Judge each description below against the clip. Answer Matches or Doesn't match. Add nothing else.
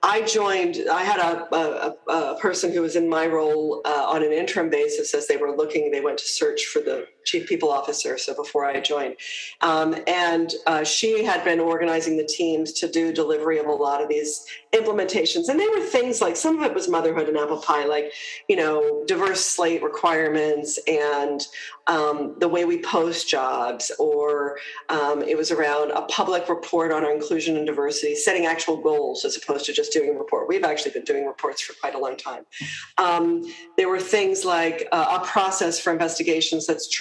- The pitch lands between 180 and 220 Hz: Doesn't match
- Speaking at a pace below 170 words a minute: Doesn't match